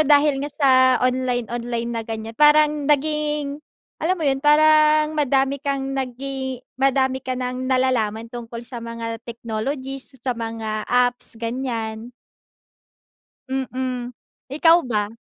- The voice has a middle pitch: No, very high, 260 Hz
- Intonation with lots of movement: No, average, 3.3 semitones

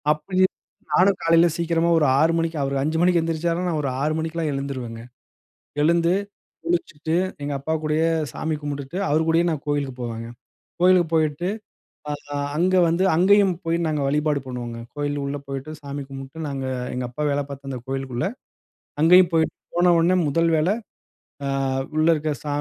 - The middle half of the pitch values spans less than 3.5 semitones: Yes, average, 3.1 semitones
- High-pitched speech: No, medium, 155 Hz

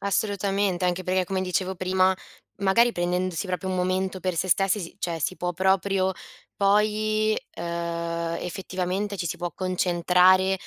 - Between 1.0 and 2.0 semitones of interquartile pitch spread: Yes, narrow, 1.5 semitones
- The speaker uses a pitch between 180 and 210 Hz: Yes, medium, 185 Hz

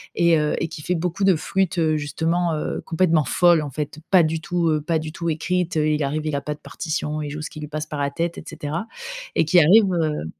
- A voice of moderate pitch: Yes, medium, 160 Hz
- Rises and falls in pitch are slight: Yes, narrow, 2.2 semitones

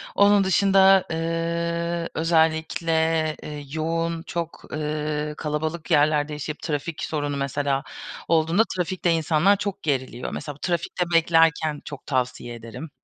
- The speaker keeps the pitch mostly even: Yes, narrow, 2.1 semitones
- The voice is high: No, medium, 160 Hz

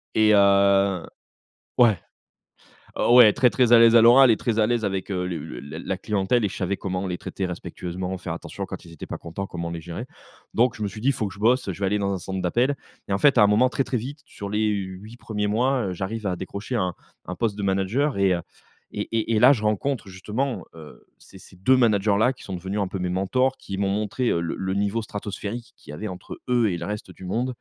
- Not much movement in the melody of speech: No, average, 3.7 semitones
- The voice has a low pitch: Yes, low, 100 Hz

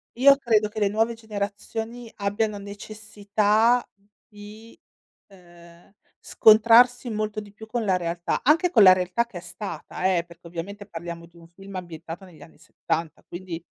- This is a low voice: No, high, 205 Hz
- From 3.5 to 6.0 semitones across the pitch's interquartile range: Yes, average, 4.0 semitones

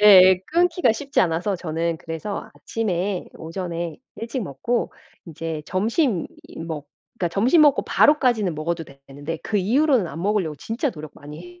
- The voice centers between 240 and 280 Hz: No, medium, 185 Hz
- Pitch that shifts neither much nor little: No, wide, 5.8 semitones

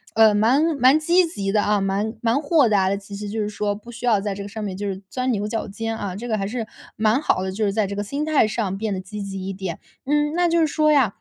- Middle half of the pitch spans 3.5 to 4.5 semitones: Yes, average, 3.9 semitones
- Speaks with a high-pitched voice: Yes, high, 215 Hz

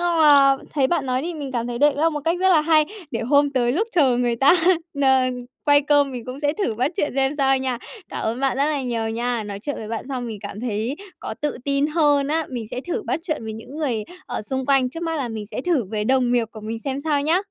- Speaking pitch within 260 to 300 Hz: Yes, very high, 270 Hz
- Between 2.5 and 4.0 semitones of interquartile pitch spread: Yes, average, 3.7 semitones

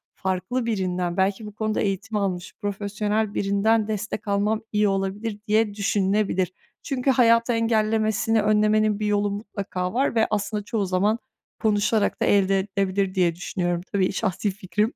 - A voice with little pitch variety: Yes, narrow, 1.9 semitones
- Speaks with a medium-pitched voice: No, high, 205 Hz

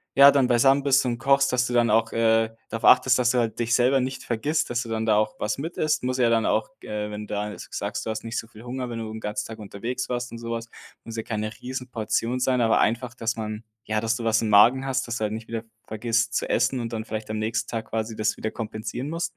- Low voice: Yes, low, 115 Hz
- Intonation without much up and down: Yes, narrow, 2.3 semitones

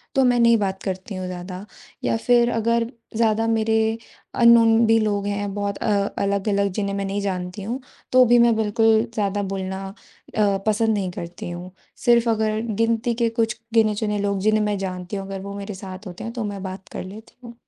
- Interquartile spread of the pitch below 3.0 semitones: Yes, narrow, 2.6 semitones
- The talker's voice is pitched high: Yes, high, 210 Hz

